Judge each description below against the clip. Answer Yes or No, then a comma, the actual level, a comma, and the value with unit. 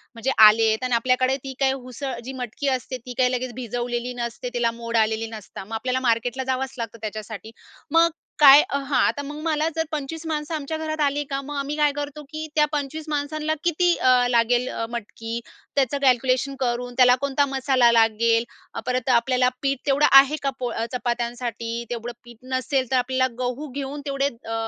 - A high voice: Yes, very high, 255 Hz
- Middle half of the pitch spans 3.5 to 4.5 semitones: No, average, 2.9 semitones